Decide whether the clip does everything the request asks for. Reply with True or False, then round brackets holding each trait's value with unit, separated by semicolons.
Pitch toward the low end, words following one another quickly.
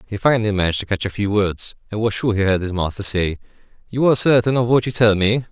True (105 Hz; 260 wpm)